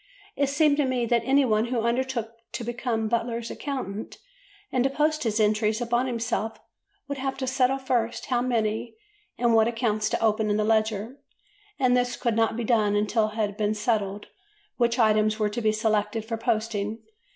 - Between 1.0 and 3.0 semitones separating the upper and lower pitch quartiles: Yes, narrow, 2.5 semitones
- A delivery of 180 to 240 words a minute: Yes, average, 185 wpm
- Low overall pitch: No, high, 230 Hz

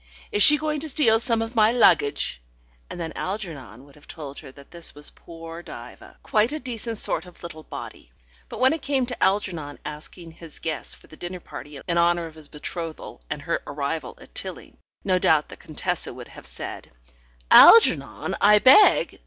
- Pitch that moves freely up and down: Yes, wide, 6.8 semitones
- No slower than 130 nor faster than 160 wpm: No, average, 190 wpm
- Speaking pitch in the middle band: Yes, medium, 170 Hz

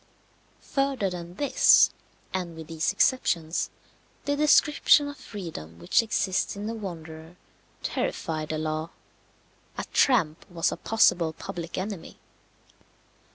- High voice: No, medium, 175 Hz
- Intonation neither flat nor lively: No, wide, 5.7 semitones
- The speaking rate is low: Yes, slow, 115 wpm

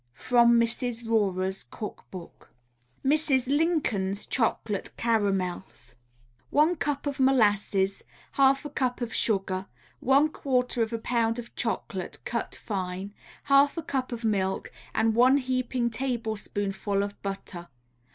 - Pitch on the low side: No, high, 230 Hz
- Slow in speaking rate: Yes, slow, 125 wpm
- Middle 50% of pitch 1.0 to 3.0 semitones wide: No, average, 4.7 semitones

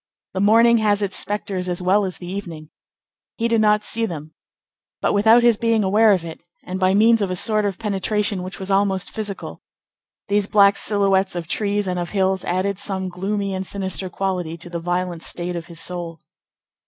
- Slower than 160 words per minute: No, average, 195 wpm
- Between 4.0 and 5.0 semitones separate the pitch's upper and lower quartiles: No, narrow, 2.5 semitones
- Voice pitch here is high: Yes, high, 195 Hz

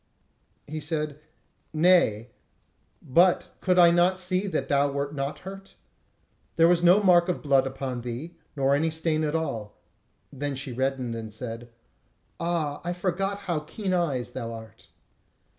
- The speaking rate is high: No, average, 155 wpm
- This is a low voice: No, medium, 150 Hz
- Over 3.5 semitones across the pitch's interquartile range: Yes, average, 4.7 semitones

